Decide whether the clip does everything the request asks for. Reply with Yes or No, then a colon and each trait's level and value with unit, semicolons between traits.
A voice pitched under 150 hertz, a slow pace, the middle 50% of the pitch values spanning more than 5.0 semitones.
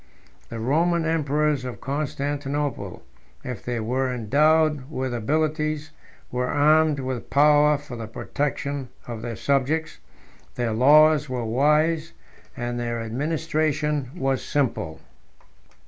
No: medium, 140 Hz; slow, 115 wpm; average, 3.6 semitones